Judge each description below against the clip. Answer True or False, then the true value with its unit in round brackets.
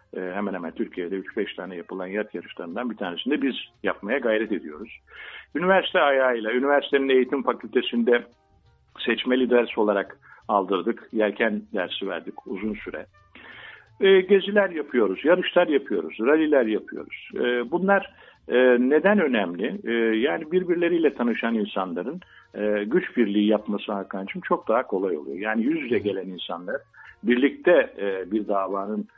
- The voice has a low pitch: True (120 Hz)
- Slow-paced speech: True (130 wpm)